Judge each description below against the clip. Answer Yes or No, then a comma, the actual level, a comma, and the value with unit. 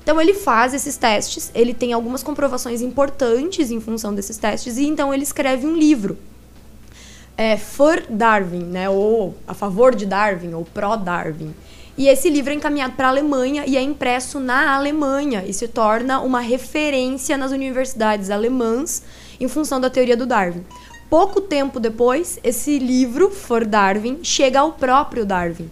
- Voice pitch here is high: Yes, very high, 255 Hz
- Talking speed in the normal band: Yes, average, 165 wpm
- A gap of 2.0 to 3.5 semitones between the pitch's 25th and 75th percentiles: No, average, 4.0 semitones